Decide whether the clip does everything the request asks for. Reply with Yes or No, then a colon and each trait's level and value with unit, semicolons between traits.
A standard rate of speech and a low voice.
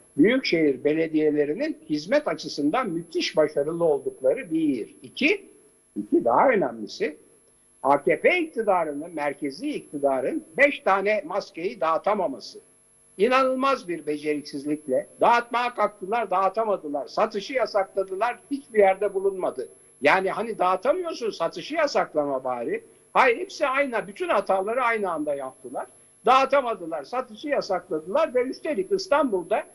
No: average, 105 wpm; high, 235 Hz